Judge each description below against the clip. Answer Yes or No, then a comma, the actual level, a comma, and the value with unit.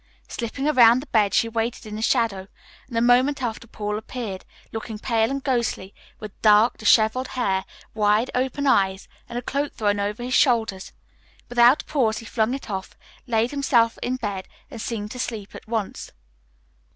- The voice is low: No, high, 230 Hz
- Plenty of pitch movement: No, average, 2.9 semitones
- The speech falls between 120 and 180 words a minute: Yes, average, 175 wpm